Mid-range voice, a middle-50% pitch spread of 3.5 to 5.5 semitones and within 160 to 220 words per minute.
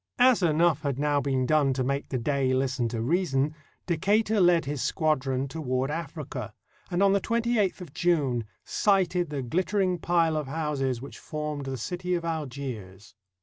Yes: medium, 150 Hz; average, 4.7 semitones; average, 165 wpm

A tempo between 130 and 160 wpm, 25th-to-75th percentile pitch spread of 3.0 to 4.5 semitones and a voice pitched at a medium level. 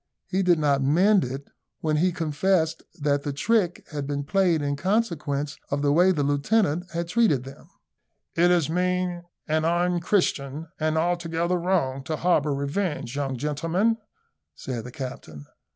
Yes: average, 150 wpm; average, 4.0 semitones; medium, 160 Hz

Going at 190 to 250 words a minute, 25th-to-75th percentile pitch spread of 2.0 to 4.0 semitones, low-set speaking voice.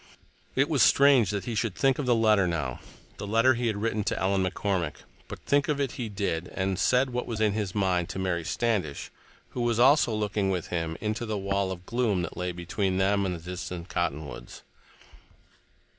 No: average, 195 wpm; average, 4.4 semitones; low, 100 Hz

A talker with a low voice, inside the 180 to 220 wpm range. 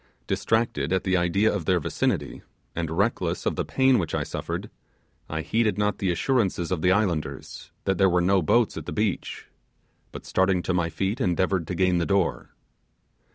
Yes: very low, 95 Hz; average, 185 wpm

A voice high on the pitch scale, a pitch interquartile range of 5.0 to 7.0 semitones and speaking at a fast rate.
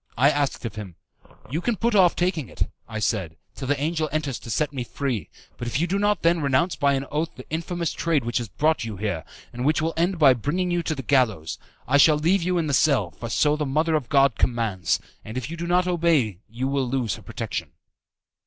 No: medium, 145 Hz; wide, 5.5 semitones; fast, 235 wpm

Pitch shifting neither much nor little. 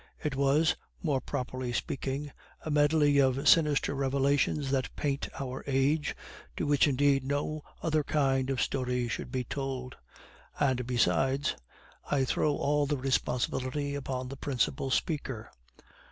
No: narrow, 1.9 semitones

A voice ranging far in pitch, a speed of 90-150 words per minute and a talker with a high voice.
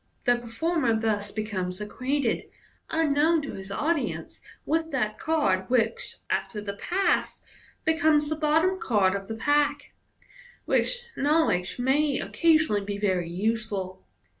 Yes: wide, 7.3 semitones; average, 140 wpm; very high, 255 Hz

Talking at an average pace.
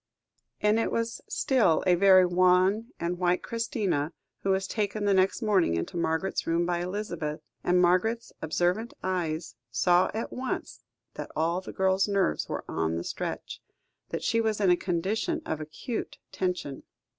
Yes: average, 160 wpm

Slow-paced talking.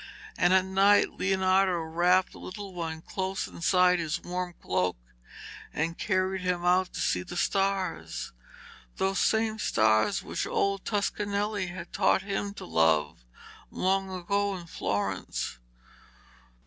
Yes: slow, 130 wpm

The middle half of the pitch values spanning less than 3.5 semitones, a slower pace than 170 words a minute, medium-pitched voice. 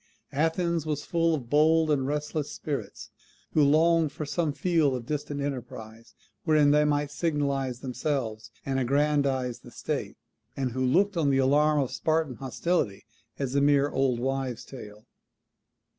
Yes: average, 2.7 semitones; average, 150 wpm; medium, 145 Hz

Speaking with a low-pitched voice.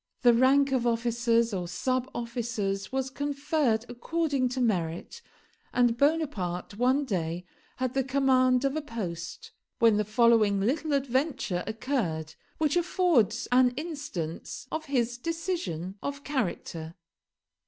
No: high, 245 Hz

